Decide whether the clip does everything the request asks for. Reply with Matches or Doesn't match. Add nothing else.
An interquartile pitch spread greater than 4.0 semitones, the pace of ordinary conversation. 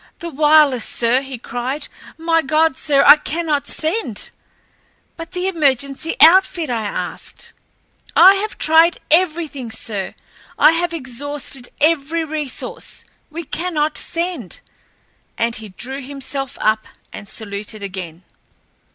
Doesn't match